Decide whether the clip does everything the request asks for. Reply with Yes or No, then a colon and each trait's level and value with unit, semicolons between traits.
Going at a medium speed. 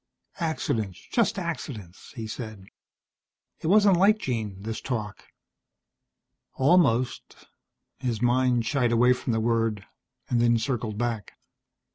No: slow, 110 wpm